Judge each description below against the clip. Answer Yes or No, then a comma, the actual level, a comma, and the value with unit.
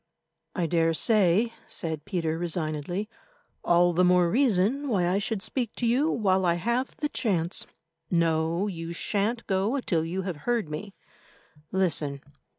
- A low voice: No, medium, 185 Hz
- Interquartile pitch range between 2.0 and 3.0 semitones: No, average, 4.6 semitones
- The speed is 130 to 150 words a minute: Yes, average, 145 wpm